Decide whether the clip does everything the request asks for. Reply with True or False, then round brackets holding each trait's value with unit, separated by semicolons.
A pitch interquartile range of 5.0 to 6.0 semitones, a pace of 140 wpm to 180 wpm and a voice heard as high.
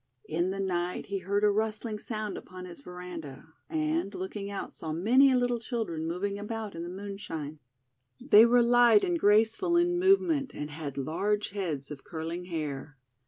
True (5.5 semitones; 175 wpm; 200 Hz)